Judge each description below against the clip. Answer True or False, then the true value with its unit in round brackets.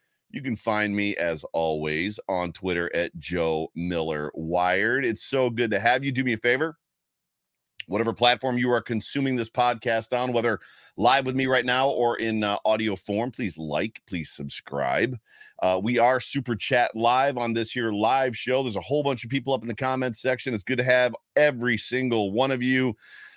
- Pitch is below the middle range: True (120 Hz)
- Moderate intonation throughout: True (4.0 semitones)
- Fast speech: False (195 wpm)